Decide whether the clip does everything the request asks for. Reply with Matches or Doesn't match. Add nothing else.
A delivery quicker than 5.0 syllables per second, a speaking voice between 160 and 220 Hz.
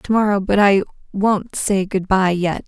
Doesn't match